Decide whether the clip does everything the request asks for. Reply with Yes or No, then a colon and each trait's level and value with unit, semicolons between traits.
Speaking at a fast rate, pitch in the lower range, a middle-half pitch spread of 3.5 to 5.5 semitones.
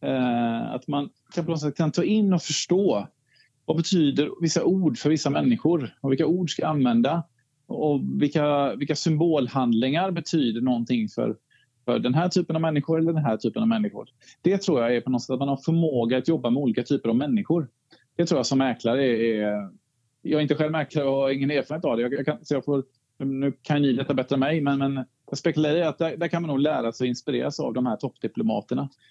No: fast, 215 wpm; medium, 145 Hz; average, 4.3 semitones